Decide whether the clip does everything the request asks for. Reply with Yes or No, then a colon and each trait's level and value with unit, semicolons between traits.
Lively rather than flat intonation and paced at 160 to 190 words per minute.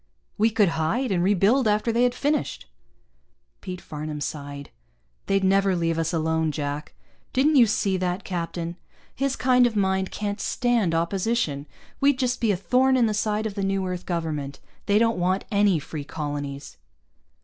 Yes: wide, 5.7 semitones; average, 170 wpm